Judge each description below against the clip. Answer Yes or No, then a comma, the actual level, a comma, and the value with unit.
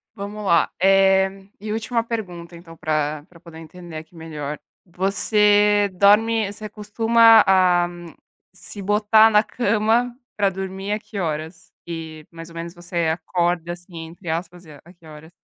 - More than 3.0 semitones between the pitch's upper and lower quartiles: Yes, average, 3.8 semitones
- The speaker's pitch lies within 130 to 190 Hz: Yes, medium, 185 Hz